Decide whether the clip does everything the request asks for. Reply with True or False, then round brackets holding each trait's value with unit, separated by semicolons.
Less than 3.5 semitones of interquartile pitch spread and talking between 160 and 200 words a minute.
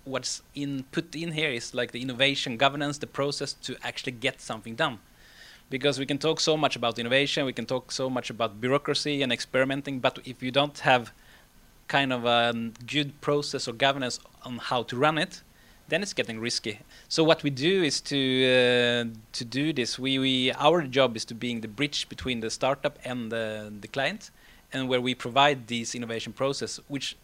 True (2.9 semitones; 195 wpm)